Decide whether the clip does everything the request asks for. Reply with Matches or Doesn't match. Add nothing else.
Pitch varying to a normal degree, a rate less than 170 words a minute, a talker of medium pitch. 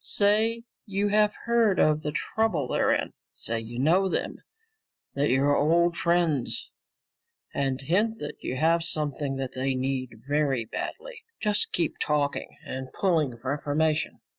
Doesn't match